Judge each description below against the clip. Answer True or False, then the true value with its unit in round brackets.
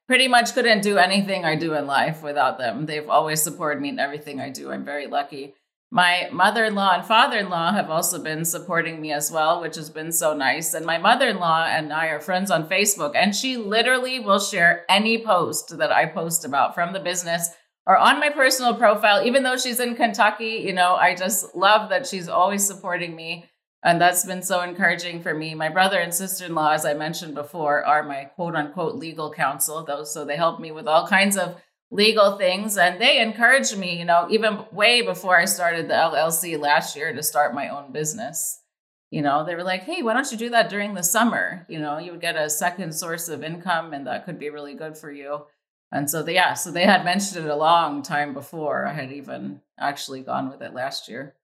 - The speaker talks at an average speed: False (225 wpm)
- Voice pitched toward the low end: False (175 Hz)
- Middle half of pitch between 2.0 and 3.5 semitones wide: False (4.4 semitones)